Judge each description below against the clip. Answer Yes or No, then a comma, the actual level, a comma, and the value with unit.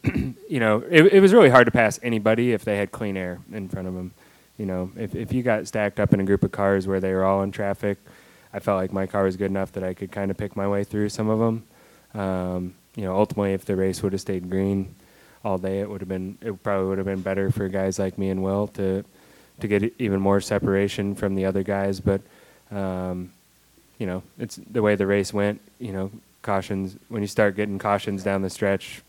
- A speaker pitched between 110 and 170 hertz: No, low, 100 Hz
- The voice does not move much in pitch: Yes, narrow, 1.4 semitones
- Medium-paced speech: No, fast, 245 wpm